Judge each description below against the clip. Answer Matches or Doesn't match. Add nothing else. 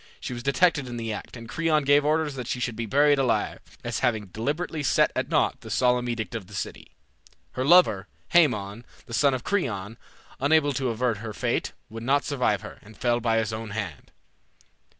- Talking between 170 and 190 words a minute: Doesn't match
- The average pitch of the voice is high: Doesn't match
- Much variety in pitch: Doesn't match